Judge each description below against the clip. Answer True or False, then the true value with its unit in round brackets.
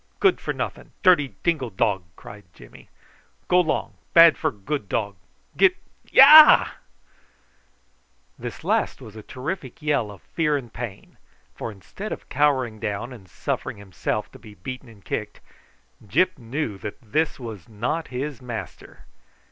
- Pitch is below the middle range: True (125 Hz)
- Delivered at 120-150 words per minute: True (145 wpm)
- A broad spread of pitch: True (6.7 semitones)